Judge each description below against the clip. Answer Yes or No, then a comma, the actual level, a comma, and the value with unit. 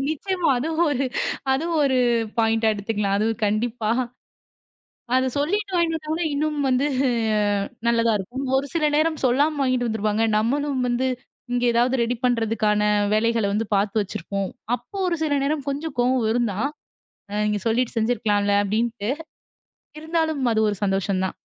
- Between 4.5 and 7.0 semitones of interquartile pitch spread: Yes, average, 4.9 semitones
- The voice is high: Yes, high, 240 Hz